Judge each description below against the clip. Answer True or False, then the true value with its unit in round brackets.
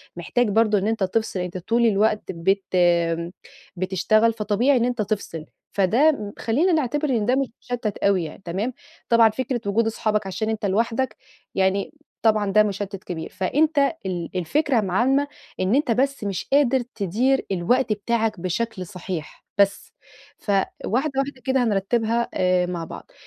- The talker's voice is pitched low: False (215 Hz)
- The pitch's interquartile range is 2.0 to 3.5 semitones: False (4.3 semitones)